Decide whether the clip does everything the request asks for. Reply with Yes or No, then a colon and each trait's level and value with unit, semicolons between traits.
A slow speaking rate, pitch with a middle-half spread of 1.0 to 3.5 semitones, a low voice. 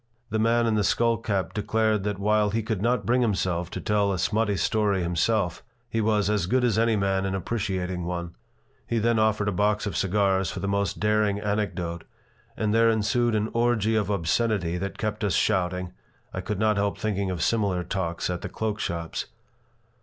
No: average, 195 wpm; narrow, 2.6 semitones; low, 105 Hz